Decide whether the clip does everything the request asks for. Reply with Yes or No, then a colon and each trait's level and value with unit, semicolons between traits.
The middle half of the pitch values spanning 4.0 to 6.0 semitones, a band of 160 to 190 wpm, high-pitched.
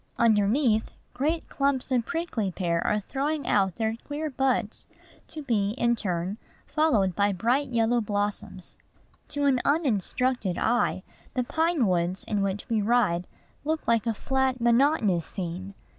No: average, 5.2 semitones; average, 145 wpm; high, 230 Hz